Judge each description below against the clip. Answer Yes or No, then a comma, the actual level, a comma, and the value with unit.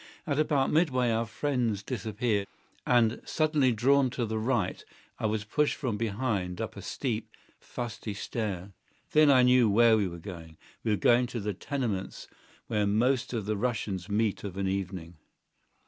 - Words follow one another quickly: No, average, 165 wpm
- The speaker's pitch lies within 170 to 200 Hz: No, low, 110 Hz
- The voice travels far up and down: No, average, 3.9 semitones